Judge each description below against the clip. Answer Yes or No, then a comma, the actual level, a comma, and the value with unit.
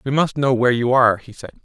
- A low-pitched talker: Yes, low, 125 Hz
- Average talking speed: No, fast, 295 wpm